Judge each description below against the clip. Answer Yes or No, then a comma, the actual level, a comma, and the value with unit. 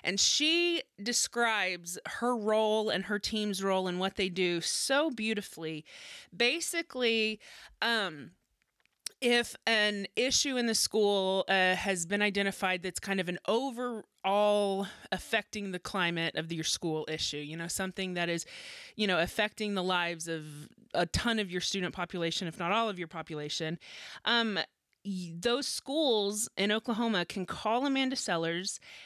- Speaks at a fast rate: No, average, 145 wpm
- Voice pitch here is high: Yes, high, 200 Hz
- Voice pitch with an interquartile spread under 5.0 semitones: Yes, average, 4.2 semitones